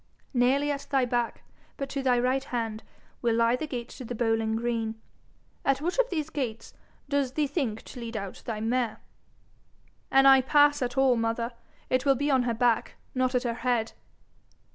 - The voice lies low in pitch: No, very high, 250 Hz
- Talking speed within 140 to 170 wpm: No, average, 185 wpm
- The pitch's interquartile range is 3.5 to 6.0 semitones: No, average, 2.7 semitones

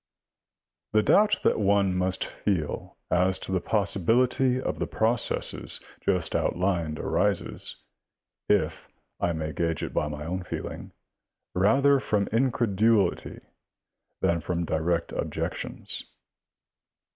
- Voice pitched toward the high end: No, very low, 95 Hz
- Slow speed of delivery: Yes, slow, 115 wpm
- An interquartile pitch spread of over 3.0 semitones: Yes, average, 4.5 semitones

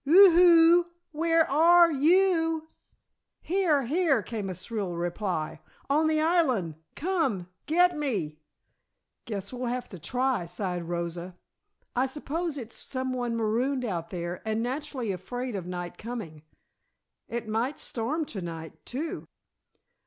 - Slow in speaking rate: Yes, slow, 130 wpm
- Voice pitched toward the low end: No, very high, 250 Hz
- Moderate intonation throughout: No, wide, 8.9 semitones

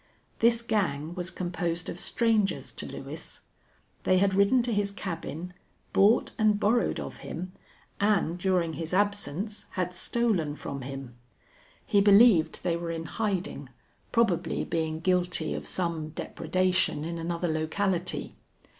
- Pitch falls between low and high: Yes, medium, 180 Hz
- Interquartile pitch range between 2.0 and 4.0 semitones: Yes, average, 3.6 semitones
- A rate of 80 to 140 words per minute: Yes, slow, 135 wpm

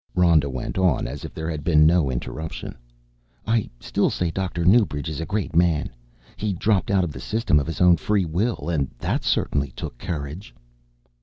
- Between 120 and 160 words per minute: No, average, 185 wpm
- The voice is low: Yes, very low, 85 Hz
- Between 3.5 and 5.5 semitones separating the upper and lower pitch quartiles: Yes, average, 4.2 semitones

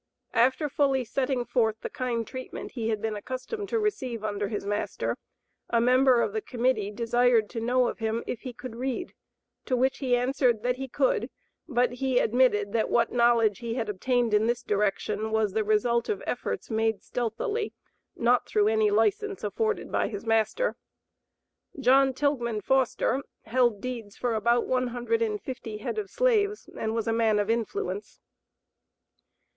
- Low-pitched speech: No, high, 240 Hz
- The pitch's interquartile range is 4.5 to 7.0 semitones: No, average, 2.8 semitones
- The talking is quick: No, average, 170 wpm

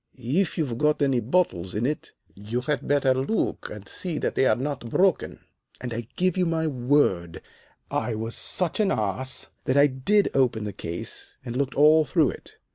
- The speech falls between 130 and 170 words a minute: No, average, 185 wpm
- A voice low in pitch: Yes, low, 130 Hz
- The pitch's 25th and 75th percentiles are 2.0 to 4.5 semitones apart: No, average, 5.0 semitones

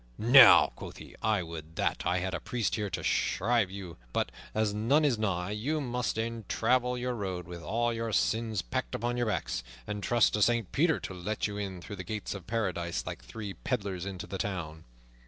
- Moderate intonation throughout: Yes, average, 4.2 semitones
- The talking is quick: Yes, fast, 210 wpm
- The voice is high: No, low, 105 Hz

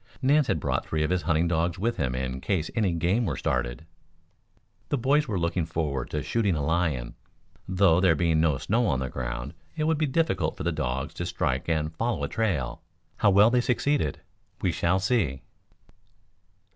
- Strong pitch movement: Yes, wide, 6.6 semitones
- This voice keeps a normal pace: Yes, average, 190 wpm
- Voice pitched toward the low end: Yes, very low, 85 Hz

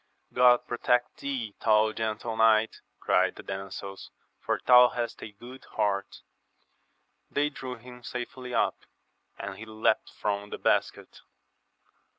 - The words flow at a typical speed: No, slow, 130 wpm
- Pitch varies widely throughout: No, average, 2.7 semitones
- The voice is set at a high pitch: No, low, 115 Hz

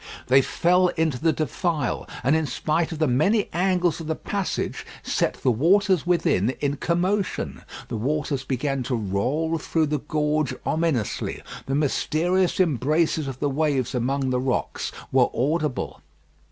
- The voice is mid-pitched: Yes, medium, 155 Hz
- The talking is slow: No, average, 150 wpm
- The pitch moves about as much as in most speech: Yes, average, 4.1 semitones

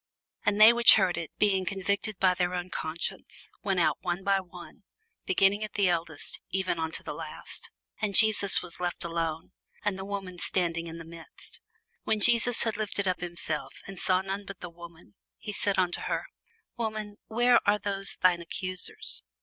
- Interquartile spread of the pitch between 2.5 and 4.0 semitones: Yes, average, 2.8 semitones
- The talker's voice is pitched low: No, high, 190 Hz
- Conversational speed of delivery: Yes, average, 180 wpm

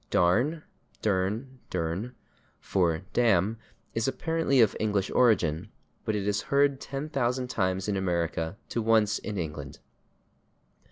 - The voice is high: No, low, 105 Hz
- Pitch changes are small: No, average, 5.3 semitones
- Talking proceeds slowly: Yes, slow, 120 wpm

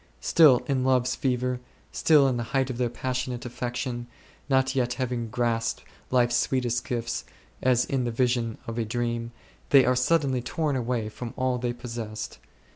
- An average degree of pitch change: No, narrow, 1.5 semitones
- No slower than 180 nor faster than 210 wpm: No, average, 165 wpm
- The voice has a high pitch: No, low, 125 Hz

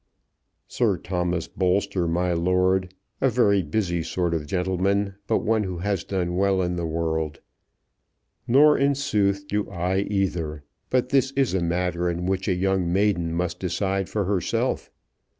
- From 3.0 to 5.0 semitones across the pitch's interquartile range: No, narrow, 2.4 semitones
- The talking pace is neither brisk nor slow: Yes, average, 155 wpm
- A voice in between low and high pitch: No, very low, 95 Hz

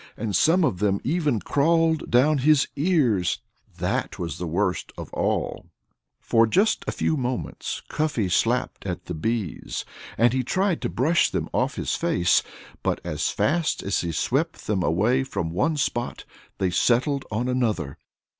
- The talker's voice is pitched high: No, low, 120 Hz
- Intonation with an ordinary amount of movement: No, wide, 7.7 semitones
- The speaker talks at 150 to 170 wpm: Yes, average, 160 wpm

